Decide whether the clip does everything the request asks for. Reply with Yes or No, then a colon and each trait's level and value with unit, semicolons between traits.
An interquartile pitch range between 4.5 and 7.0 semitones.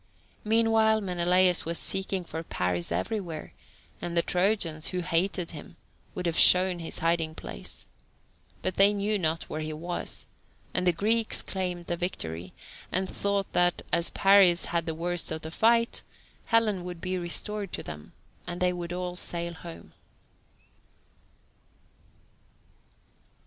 No: average, 2.7 semitones